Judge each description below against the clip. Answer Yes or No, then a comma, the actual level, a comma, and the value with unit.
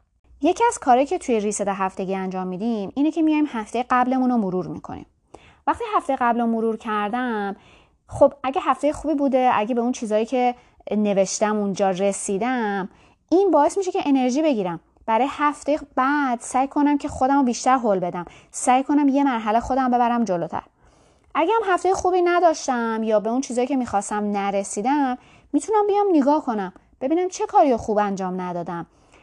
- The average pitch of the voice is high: Yes, very high, 250 Hz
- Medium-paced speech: No, fast, 170 wpm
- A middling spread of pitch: No, wide, 5.8 semitones